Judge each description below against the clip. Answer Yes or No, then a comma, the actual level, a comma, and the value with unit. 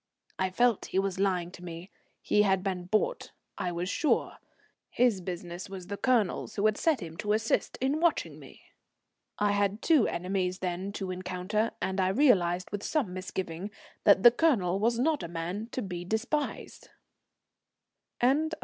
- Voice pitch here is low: No, high, 195 Hz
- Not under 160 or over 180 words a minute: Yes, average, 170 wpm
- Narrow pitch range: No, average, 4.0 semitones